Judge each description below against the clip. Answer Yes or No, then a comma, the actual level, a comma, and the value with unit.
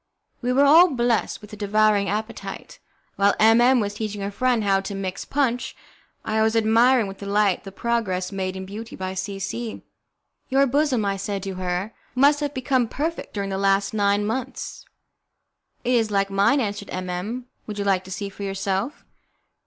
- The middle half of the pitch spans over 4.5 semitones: No, average, 3.5 semitones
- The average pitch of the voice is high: Yes, high, 210 Hz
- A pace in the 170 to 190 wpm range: Yes, average, 185 wpm